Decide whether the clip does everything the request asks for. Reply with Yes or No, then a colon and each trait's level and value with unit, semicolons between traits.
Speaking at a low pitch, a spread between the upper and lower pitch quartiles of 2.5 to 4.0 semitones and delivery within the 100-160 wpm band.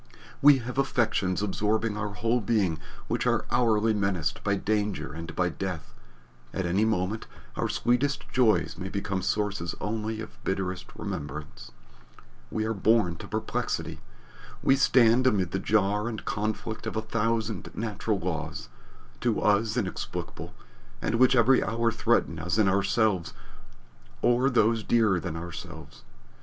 Yes: low, 105 Hz; average, 3.6 semitones; average, 140 wpm